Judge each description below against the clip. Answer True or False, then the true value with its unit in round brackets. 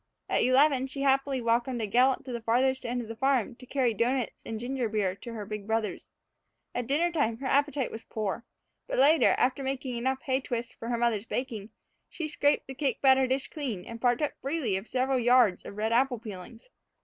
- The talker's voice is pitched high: True (250 Hz)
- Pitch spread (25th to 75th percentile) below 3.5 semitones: True (2.9 semitones)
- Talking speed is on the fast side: True (210 wpm)